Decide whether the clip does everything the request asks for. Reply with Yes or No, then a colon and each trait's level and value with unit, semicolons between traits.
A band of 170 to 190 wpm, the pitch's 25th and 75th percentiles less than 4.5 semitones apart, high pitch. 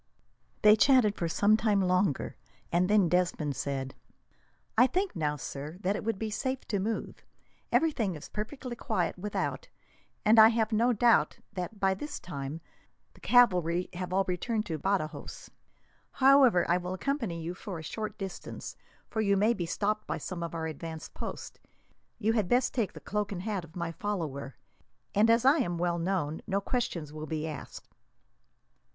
No: average, 175 wpm; average, 4.8 semitones; high, 195 Hz